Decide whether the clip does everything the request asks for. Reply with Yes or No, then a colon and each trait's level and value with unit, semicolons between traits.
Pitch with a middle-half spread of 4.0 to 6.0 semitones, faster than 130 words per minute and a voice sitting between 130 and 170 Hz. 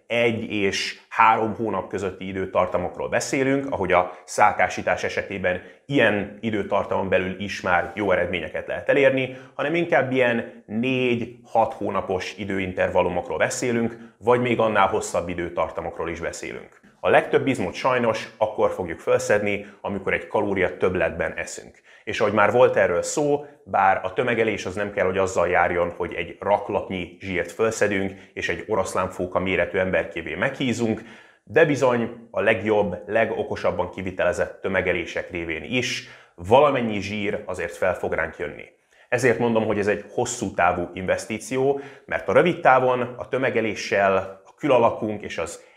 No: average, 4.5 semitones; average, 140 wpm; low, 115 Hz